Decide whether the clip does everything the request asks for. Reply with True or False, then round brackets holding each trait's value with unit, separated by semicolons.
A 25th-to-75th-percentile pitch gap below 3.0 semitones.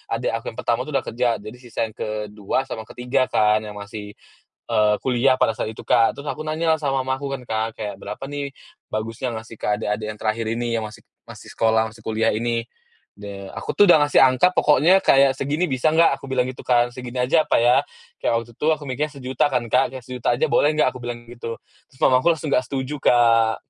False (3.4 semitones)